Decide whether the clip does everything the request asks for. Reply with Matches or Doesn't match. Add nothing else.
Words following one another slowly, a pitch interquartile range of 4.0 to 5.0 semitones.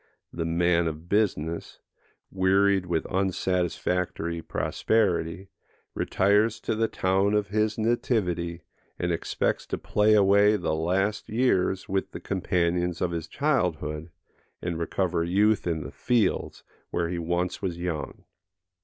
Doesn't match